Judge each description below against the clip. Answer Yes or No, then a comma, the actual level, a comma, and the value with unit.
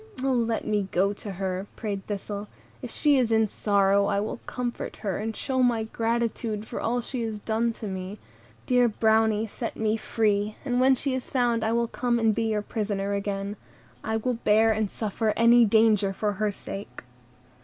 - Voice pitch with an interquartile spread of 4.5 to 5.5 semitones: No, narrow, 2.4 semitones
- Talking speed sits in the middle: Yes, average, 190 wpm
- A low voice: No, high, 220 Hz